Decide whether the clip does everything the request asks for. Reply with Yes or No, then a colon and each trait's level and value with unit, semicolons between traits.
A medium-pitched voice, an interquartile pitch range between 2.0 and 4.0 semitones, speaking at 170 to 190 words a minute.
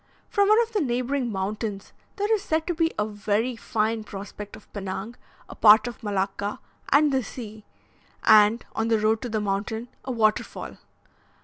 No: high, 220 Hz; average, 3.7 semitones; average, 175 wpm